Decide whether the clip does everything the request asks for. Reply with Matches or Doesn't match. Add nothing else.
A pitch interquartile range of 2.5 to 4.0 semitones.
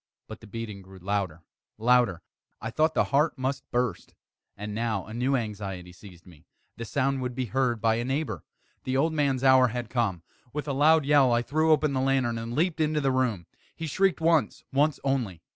Doesn't match